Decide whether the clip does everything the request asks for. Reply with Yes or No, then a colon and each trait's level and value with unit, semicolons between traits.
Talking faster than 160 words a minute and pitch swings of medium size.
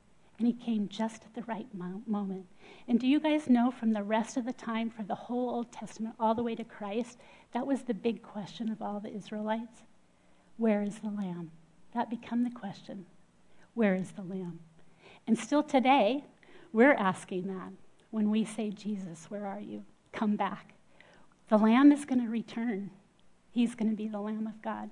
Yes: average, 190 wpm; average, 3.0 semitones